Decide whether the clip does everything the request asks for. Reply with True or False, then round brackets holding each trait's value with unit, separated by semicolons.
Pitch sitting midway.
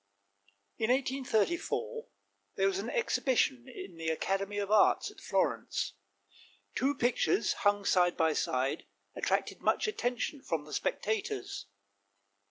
False (220 Hz)